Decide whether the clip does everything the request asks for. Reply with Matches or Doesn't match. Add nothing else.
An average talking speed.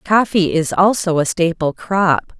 Matches